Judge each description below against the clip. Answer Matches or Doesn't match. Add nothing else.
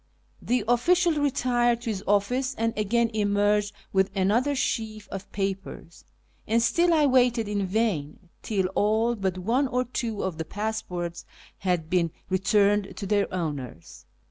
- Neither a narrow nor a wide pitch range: Matches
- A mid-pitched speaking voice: Doesn't match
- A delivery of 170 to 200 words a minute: Doesn't match